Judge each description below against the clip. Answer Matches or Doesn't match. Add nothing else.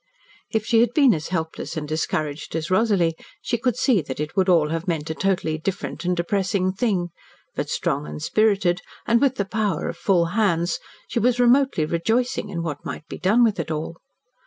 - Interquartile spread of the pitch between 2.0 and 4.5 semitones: Doesn't match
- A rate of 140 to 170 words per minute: Doesn't match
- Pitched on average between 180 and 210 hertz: Matches